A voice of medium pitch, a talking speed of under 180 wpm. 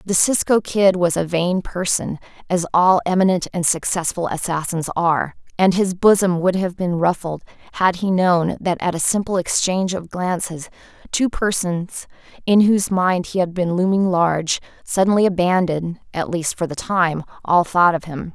Yes: medium, 180 Hz; average, 170 wpm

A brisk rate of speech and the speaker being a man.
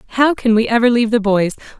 No: fast, 235 wpm; female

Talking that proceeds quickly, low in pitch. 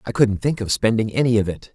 Yes: fast, 275 wpm; low, 110 Hz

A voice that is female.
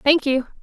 Yes: female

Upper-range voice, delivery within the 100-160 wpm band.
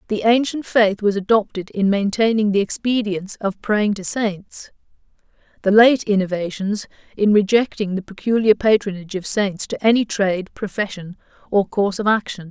Yes: high, 205 Hz; average, 150 wpm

